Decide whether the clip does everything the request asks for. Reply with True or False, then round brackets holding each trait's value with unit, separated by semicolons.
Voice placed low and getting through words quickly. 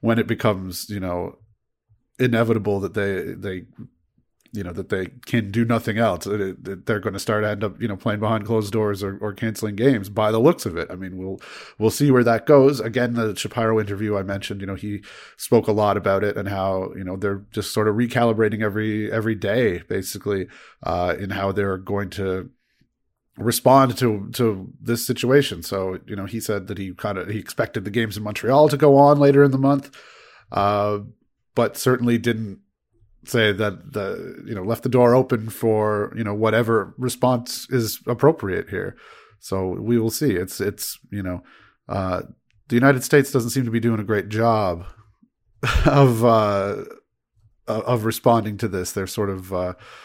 False (110 Hz; 190 wpm)